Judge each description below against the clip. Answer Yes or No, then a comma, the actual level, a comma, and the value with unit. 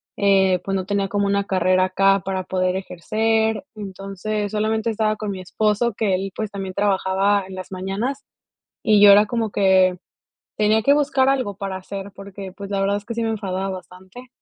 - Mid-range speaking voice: No, high, 200 Hz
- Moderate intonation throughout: No, narrow, 2.2 semitones